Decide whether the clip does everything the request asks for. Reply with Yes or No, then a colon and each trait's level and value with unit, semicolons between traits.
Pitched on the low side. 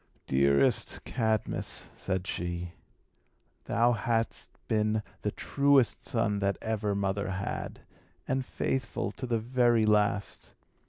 Yes: low, 110 Hz